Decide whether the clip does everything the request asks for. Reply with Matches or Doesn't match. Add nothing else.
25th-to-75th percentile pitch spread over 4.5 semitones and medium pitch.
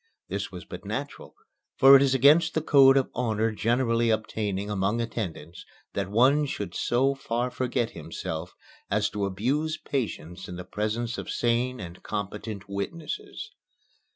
Doesn't match